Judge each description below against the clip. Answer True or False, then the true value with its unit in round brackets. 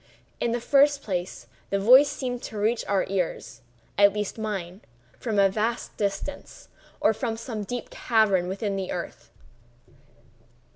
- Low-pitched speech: False (210 Hz)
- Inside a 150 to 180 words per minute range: False (135 wpm)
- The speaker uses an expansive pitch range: False (3.5 semitones)